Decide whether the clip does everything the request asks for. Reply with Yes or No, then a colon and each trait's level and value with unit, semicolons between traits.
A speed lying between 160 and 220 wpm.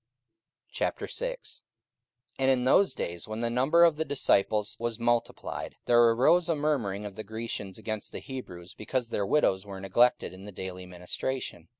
Yes: average, 165 wpm